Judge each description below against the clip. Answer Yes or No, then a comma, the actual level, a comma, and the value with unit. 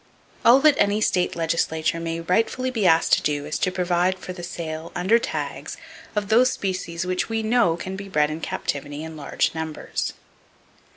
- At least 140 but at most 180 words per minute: No, average, 190 wpm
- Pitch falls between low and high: Yes, medium, 180 Hz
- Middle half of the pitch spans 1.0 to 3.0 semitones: No, average, 4.1 semitones